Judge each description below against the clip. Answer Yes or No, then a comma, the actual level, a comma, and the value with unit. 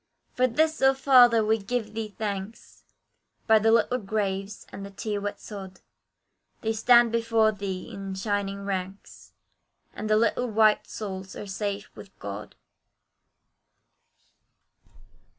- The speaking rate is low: Yes, slow, 130 wpm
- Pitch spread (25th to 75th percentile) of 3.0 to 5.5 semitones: No, narrow, 2.5 semitones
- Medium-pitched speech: No, high, 210 Hz